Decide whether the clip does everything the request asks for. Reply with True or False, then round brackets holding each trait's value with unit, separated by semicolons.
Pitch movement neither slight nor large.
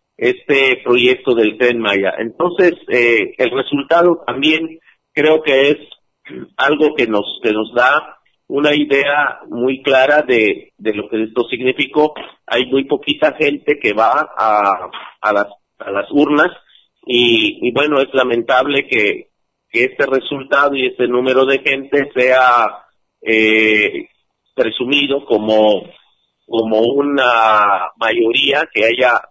True (4.3 semitones)